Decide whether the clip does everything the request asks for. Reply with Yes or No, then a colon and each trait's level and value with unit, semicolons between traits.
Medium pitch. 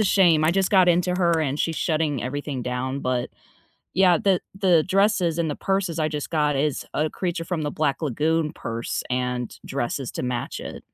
Yes: medium, 155 Hz